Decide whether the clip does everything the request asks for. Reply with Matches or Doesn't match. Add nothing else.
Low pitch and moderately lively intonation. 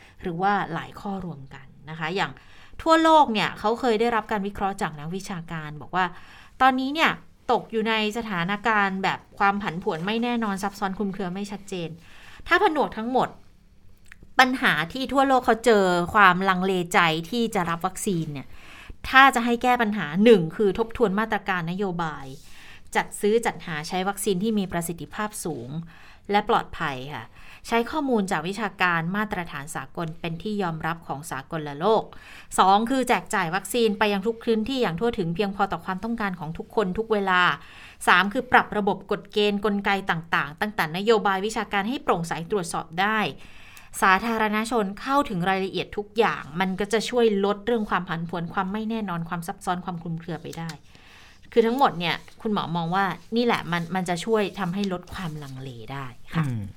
Doesn't match